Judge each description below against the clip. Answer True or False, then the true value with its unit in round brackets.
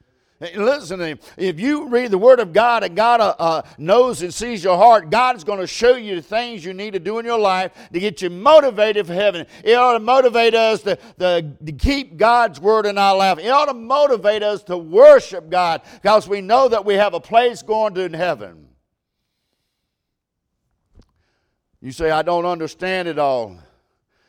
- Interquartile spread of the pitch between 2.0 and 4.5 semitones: False (5.0 semitones)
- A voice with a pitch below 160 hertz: False (205 Hz)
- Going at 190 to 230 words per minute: True (200 wpm)